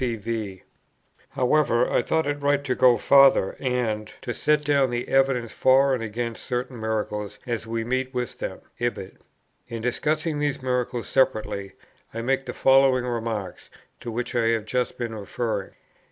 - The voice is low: Yes, low, 120 Hz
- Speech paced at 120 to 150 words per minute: No, average, 160 wpm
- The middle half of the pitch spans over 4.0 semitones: No, average, 2.9 semitones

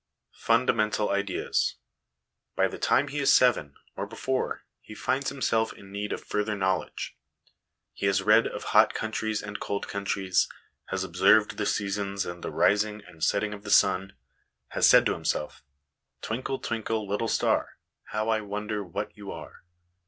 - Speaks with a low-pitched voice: Yes, low, 105 Hz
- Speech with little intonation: Yes, narrow, 1.8 semitones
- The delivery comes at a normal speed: Yes, average, 160 wpm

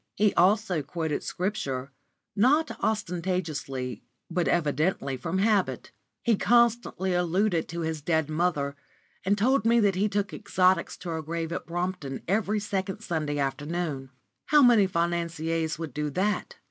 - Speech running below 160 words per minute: Yes, average, 140 wpm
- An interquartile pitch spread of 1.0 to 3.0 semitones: No, average, 4.4 semitones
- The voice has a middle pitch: Yes, medium, 175 Hz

